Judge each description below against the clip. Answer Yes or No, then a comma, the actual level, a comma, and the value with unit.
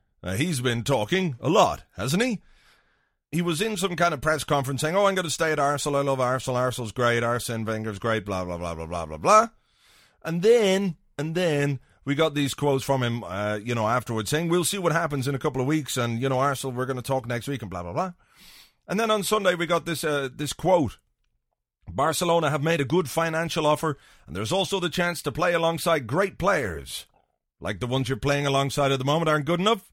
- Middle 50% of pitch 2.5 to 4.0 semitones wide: No, average, 5.3 semitones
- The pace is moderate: No, fast, 235 wpm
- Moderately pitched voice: Yes, medium, 145 Hz